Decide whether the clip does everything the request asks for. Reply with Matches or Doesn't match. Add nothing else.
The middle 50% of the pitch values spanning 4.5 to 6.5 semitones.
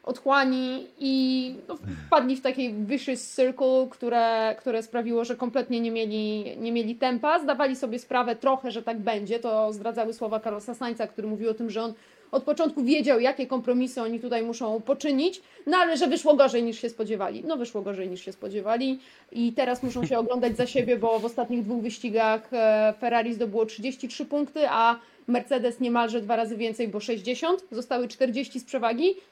Doesn't match